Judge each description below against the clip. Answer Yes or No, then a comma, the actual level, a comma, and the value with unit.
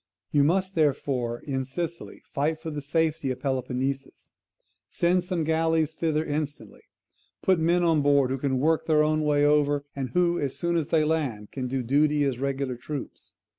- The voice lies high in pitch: No, medium, 150 Hz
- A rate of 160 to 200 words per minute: Yes, average, 175 wpm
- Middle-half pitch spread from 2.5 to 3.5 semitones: Yes, average, 3.0 semitones